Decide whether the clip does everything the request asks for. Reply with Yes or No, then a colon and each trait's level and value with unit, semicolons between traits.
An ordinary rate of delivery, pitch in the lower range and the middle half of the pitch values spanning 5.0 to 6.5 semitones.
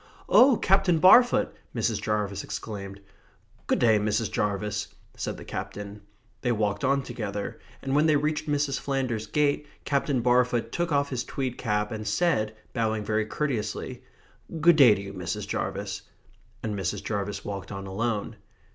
Yes: average, 155 wpm; low, 110 Hz; average, 5.3 semitones